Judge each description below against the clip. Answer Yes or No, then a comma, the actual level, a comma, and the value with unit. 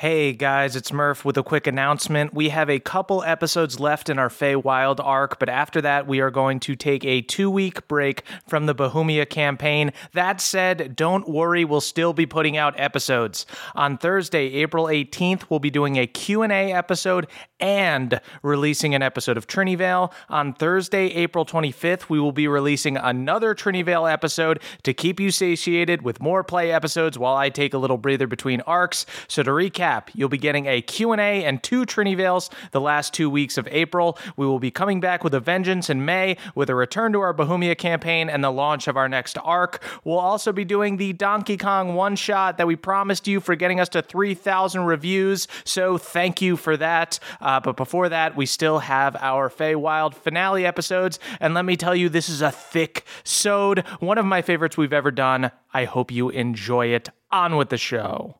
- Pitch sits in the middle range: Yes, medium, 160 Hz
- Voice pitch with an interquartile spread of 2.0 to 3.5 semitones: No, average, 4.5 semitones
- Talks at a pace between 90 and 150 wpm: No, average, 190 wpm